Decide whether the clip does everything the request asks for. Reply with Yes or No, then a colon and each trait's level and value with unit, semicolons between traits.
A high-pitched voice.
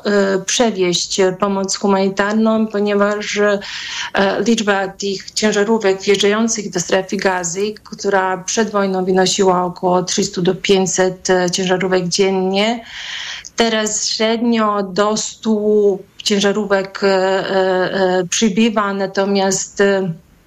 Yes: high, 195 Hz